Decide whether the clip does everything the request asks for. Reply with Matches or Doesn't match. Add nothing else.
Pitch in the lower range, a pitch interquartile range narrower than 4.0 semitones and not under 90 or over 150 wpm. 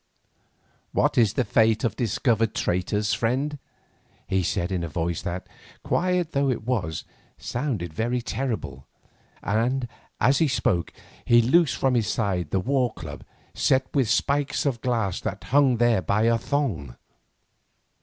Doesn't match